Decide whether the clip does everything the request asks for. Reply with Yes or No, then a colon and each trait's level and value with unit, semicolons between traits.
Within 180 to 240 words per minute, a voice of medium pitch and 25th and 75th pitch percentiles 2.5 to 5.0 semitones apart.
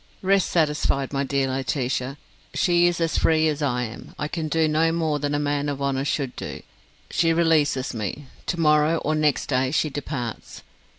Yes: average, 185 wpm; medium, 145 Hz; average, 2.9 semitones